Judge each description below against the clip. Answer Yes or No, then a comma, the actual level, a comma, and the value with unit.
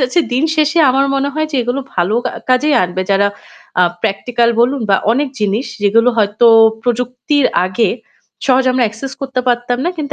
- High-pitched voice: Yes, very high, 250 Hz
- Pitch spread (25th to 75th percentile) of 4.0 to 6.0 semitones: No, average, 3.6 semitones